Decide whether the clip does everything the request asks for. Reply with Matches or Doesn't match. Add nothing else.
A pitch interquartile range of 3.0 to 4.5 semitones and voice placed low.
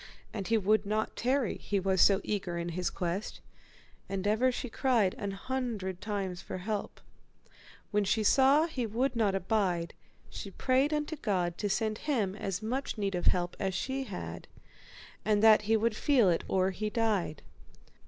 Doesn't match